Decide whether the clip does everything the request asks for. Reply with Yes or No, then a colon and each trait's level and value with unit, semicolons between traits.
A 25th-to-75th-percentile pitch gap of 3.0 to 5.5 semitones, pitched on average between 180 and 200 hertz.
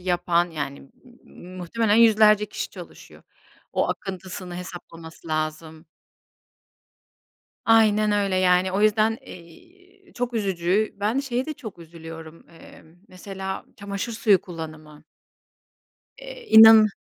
Yes: average, 4.5 semitones; high, 190 Hz